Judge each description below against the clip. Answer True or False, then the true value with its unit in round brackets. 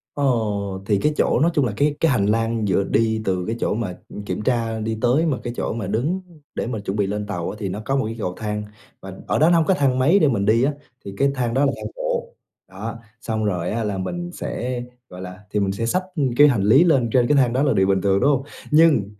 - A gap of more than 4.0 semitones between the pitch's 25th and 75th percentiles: True (5.5 semitones)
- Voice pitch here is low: True (115 Hz)